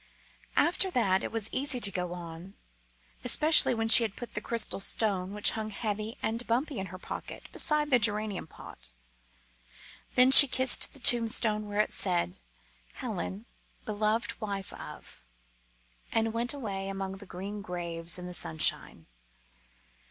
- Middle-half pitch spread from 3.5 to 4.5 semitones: Yes, average, 4.2 semitones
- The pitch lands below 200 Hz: No, high, 210 Hz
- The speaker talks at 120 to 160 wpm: Yes, average, 150 wpm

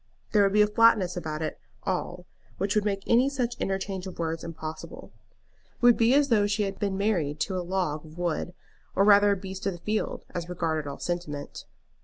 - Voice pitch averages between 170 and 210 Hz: Yes, high, 190 Hz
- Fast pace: Yes, fast, 210 wpm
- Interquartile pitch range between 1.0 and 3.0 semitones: No, average, 3.4 semitones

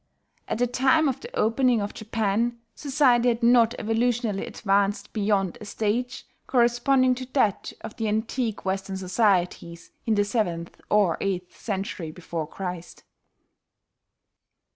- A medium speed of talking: No, slow, 130 wpm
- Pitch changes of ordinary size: Yes, average, 3.8 semitones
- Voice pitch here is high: Yes, high, 220 Hz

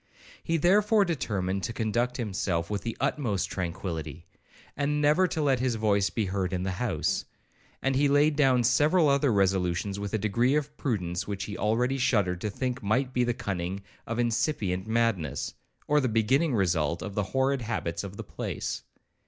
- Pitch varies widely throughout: Yes, wide, 5.7 semitones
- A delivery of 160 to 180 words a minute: Yes, average, 175 wpm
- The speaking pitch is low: Yes, low, 115 Hz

